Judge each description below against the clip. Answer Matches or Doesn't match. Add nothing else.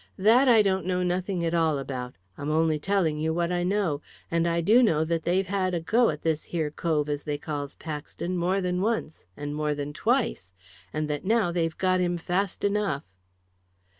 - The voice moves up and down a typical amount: Matches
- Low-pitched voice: Doesn't match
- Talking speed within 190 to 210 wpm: Matches